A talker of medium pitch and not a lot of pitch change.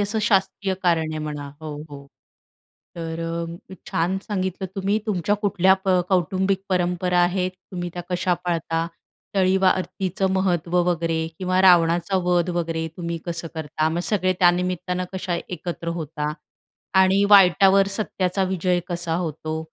Yes: medium, 180 Hz; narrow, 2.2 semitones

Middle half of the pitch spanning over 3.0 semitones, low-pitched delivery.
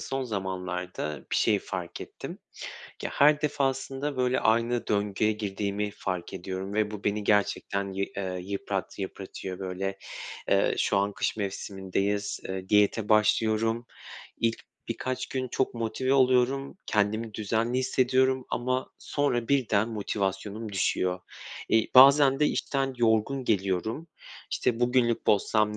Yes: average, 4.4 semitones; low, 110 Hz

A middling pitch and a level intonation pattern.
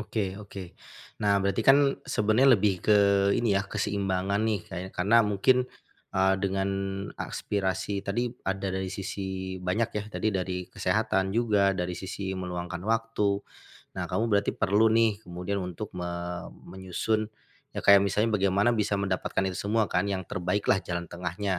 No: low, 100 Hz; narrow, 2.1 semitones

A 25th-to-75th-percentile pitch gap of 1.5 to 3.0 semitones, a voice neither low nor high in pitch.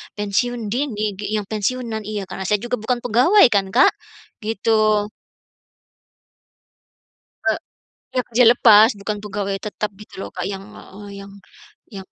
No: narrow, 2.6 semitones; high, 215 Hz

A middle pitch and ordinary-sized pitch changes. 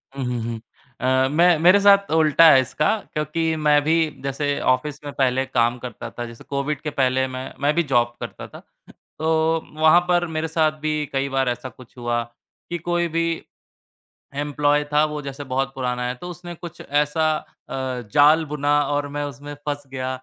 Yes: medium, 145 Hz; average, 3.4 semitones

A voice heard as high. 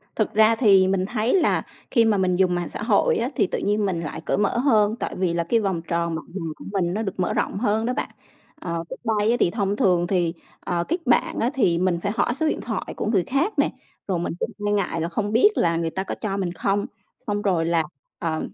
Yes: high, 195 Hz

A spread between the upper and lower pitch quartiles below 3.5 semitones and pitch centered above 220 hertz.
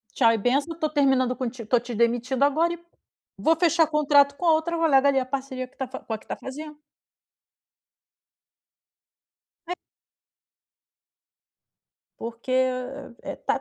Yes: average, 3.1 semitones; very high, 270 Hz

